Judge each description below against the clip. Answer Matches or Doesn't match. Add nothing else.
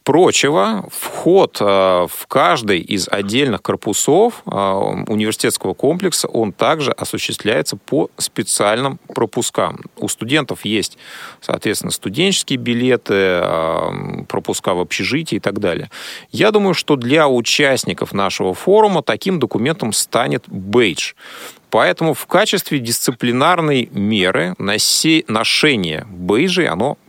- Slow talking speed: Matches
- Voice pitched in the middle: Doesn't match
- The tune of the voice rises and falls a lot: Matches